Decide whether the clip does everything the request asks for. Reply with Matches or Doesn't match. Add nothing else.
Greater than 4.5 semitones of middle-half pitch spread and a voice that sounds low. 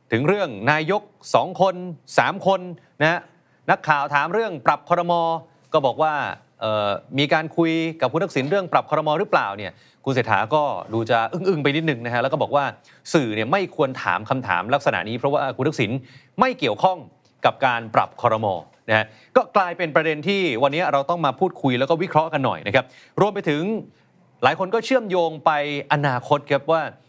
Doesn't match